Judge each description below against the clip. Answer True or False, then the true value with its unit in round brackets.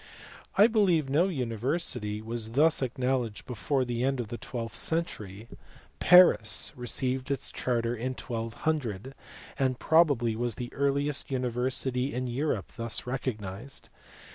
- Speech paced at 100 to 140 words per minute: True (135 wpm)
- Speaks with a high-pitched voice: False (125 Hz)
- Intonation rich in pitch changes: False (3.3 semitones)